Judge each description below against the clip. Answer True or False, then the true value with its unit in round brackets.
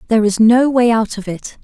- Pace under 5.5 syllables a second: False (5.6 syllables/s)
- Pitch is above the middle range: True (225 Hz)